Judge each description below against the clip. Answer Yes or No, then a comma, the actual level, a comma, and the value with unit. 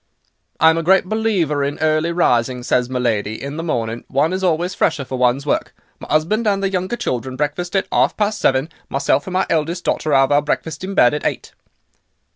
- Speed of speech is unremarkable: No, fast, 210 wpm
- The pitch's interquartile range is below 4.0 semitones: No, wide, 5.5 semitones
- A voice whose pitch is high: No, medium, 155 Hz